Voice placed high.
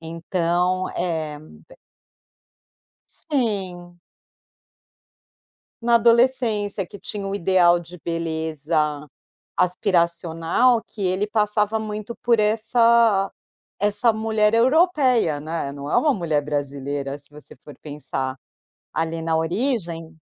No: medium, 180 Hz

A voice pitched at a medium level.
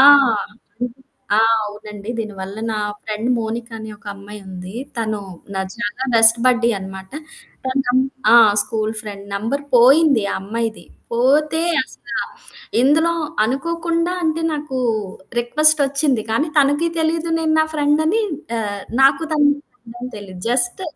No: high, 240 Hz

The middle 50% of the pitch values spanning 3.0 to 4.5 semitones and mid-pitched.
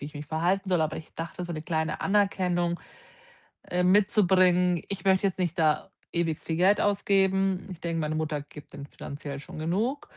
Yes: average, 3.4 semitones; medium, 175 Hz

